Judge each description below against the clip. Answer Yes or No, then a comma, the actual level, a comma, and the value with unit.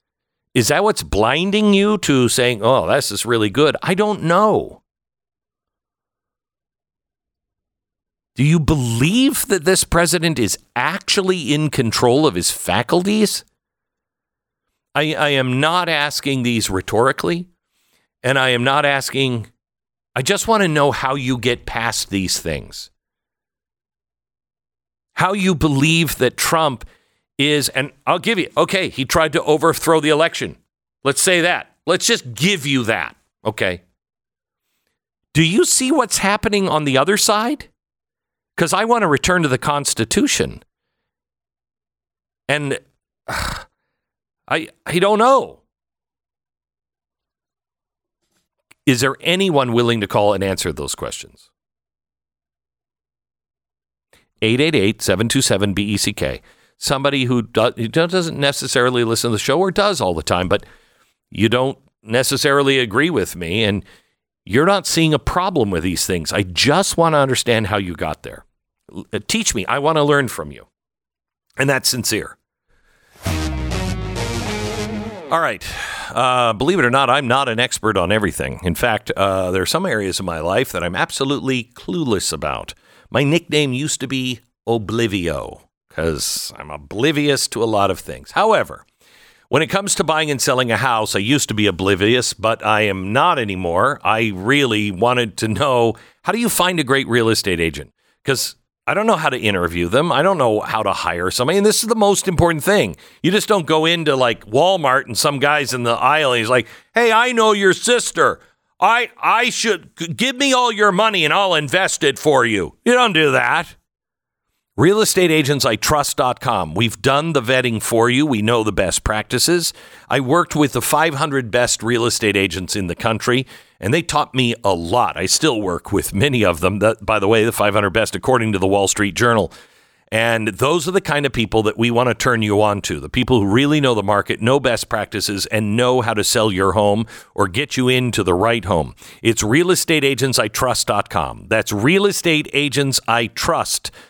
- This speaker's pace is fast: No, average, 165 wpm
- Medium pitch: No, low, 125 Hz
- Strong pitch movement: Yes, wide, 7.2 semitones